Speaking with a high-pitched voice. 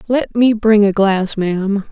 Yes: high, 210 Hz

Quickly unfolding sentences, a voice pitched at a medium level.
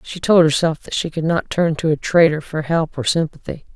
Yes: fast, 240 wpm; medium, 160 Hz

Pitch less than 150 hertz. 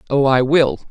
Yes: medium, 140 Hz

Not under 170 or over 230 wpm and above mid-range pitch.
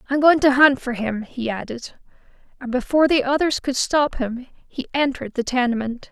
Yes: average, 185 wpm; very high, 260 Hz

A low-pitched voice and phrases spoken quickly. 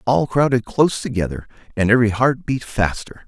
No: low, 120 Hz; average, 165 wpm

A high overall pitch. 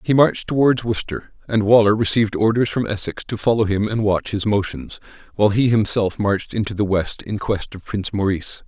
No: low, 105 Hz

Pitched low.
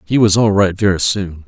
Yes: low, 100 Hz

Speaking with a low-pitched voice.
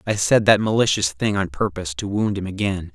Yes: low, 100 Hz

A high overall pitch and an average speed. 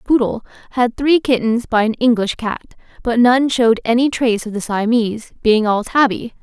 Yes: high, 235 Hz; average, 175 wpm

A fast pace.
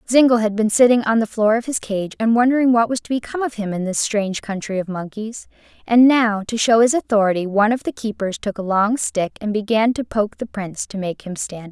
Yes: fast, 250 wpm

